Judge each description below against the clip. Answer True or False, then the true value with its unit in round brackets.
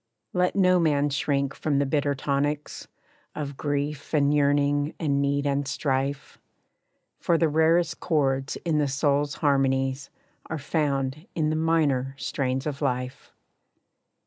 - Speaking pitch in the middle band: True (145 Hz)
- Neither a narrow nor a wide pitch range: False (1.8 semitones)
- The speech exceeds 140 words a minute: False (135 wpm)